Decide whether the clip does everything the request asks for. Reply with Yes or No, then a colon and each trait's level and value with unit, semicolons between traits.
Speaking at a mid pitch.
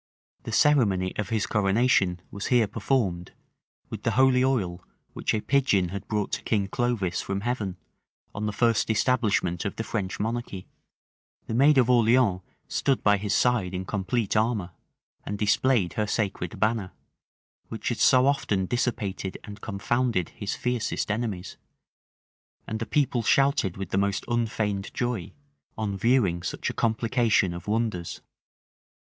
No: low, 105 Hz